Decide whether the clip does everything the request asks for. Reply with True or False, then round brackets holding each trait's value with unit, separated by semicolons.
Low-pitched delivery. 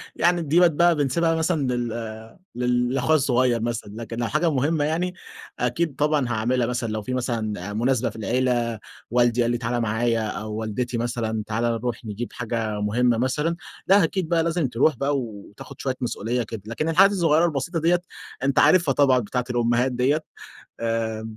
True (125 Hz)